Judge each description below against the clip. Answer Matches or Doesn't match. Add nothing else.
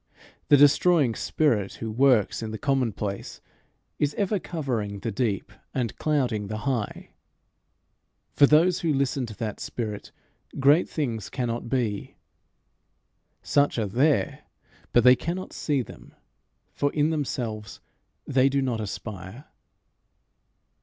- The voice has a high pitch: Doesn't match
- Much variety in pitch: Doesn't match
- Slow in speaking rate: Matches